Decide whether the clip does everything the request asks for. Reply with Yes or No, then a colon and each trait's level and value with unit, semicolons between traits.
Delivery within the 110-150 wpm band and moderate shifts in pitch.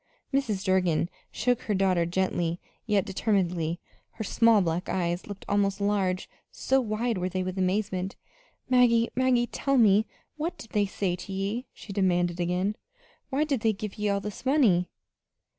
No: average, 160 wpm; average, 3.7 semitones